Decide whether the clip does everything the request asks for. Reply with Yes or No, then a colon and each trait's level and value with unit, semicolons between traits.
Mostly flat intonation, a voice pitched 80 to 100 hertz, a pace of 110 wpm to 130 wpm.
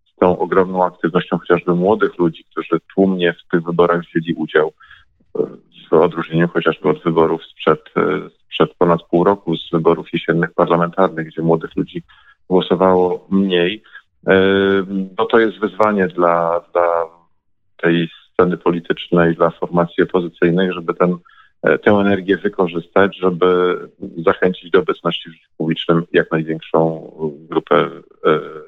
Yes: narrow, 2.1 semitones; very low, 90 Hz; average, 125 wpm